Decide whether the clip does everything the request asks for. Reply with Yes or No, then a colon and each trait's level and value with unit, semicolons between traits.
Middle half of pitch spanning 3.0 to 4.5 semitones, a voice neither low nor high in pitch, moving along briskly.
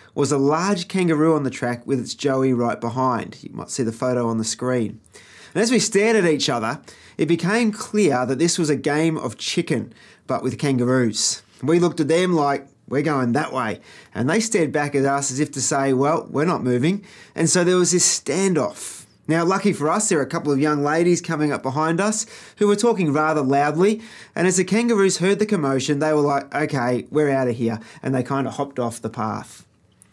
No: wide, 5.4 semitones; medium, 150 Hz; fast, 225 wpm